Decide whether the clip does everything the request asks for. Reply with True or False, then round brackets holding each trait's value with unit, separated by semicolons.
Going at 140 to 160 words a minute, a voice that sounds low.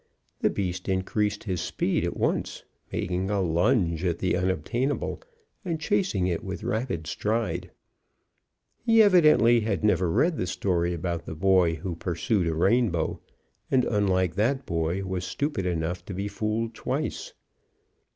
True (145 wpm; 95 Hz)